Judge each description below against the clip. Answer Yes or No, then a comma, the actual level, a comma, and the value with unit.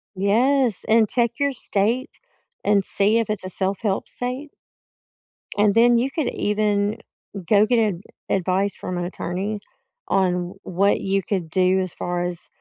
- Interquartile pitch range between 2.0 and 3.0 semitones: No, average, 3.6 semitones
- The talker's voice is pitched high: Yes, high, 205 Hz